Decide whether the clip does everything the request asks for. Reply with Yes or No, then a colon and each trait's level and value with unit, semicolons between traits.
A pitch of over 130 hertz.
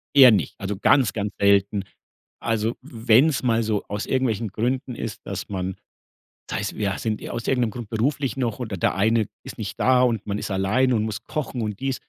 No: low, 110 Hz